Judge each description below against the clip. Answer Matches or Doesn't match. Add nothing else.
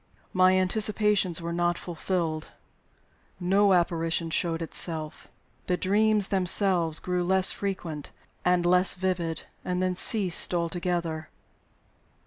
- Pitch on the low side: Doesn't match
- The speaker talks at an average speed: Doesn't match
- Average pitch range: Doesn't match